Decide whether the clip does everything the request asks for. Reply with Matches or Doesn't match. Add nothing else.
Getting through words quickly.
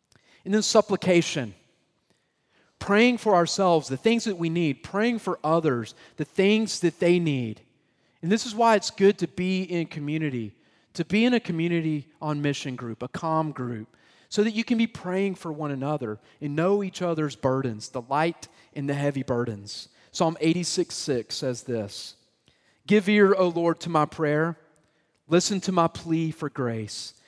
Doesn't match